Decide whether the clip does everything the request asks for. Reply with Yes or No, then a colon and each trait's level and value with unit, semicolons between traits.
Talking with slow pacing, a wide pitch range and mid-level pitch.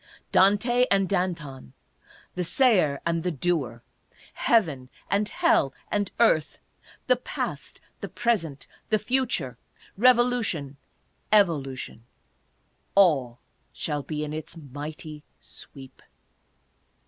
Yes: slow, 105 wpm; wide, 6.6 semitones; medium, 165 Hz